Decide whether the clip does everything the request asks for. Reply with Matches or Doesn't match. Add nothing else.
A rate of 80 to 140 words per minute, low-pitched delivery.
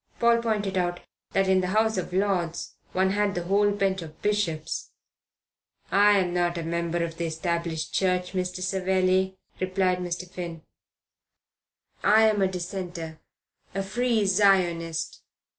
Doesn't match